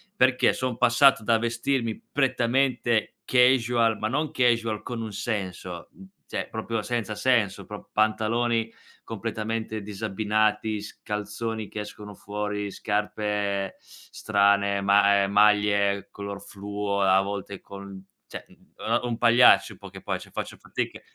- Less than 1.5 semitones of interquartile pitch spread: No, narrow, 2.4 semitones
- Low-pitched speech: Yes, low, 110 Hz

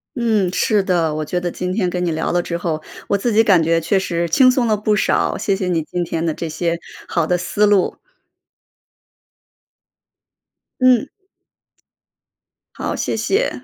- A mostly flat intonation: No, average, 3.9 semitones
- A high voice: No, medium, 180 Hz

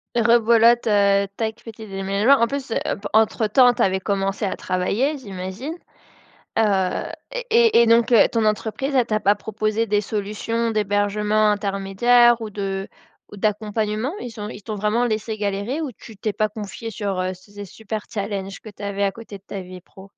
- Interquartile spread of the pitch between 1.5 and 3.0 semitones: Yes, narrow, 2.4 semitones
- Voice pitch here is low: No, high, 215 Hz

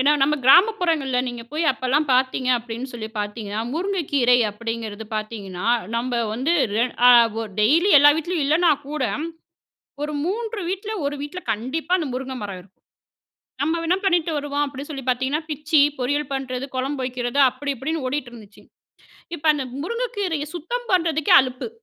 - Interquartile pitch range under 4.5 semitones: No, average, 4.8 semitones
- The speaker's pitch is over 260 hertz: Yes, very high, 280 Hz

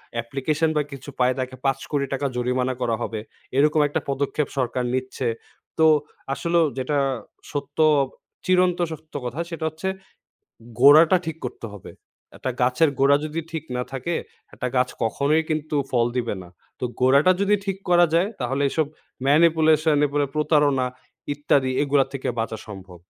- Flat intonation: No, average, 3.6 semitones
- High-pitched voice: No, medium, 140 Hz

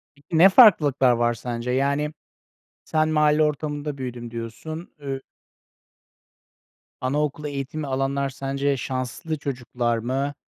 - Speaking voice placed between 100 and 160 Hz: Yes, medium, 140 Hz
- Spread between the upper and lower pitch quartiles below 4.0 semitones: Yes, average, 3.0 semitones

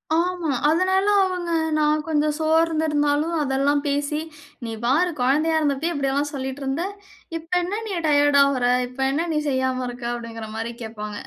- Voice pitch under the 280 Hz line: No, very high, 290 Hz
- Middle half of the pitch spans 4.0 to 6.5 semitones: No, average, 3.4 semitones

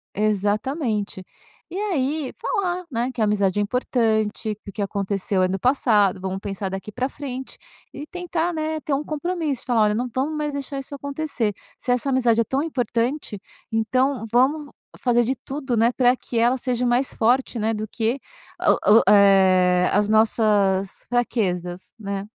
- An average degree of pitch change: Yes, average, 4.9 semitones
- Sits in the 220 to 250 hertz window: Yes, high, 240 Hz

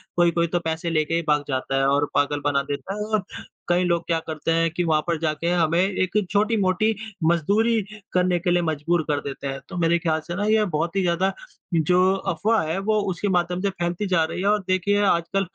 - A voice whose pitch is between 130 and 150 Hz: No, medium, 175 Hz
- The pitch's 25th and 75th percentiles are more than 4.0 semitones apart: No, average, 3.1 semitones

